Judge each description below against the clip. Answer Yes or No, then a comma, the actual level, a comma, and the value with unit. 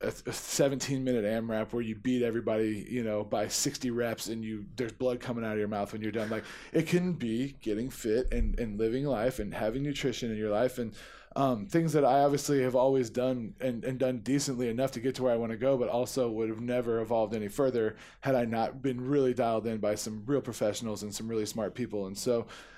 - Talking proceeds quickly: Yes, fast, 230 wpm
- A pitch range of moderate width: Yes, average, 3.0 semitones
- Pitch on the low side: Yes, low, 120 Hz